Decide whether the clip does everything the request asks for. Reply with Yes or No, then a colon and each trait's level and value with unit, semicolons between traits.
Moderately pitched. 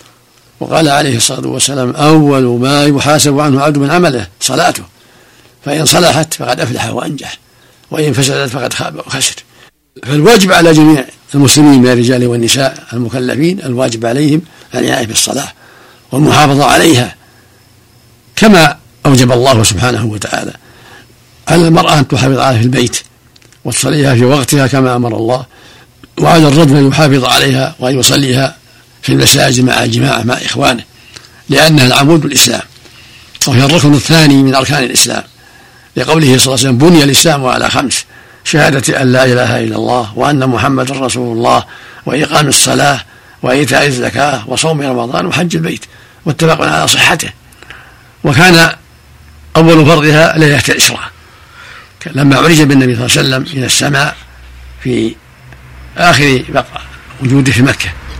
No: low, 130 Hz